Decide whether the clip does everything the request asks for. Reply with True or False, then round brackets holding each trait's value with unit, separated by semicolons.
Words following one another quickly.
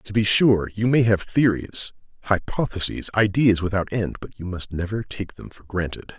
False (185 wpm)